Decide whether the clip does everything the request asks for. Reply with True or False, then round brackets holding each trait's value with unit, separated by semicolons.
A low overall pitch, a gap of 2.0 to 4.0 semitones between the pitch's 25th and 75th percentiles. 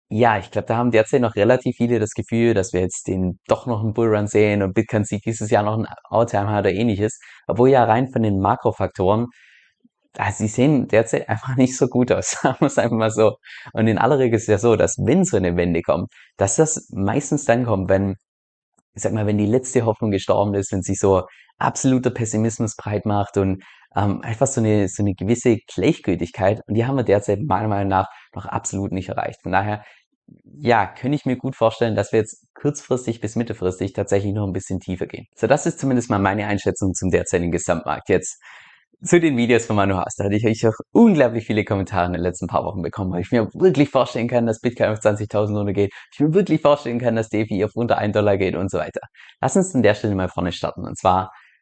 True (105 Hz; 3.3 semitones)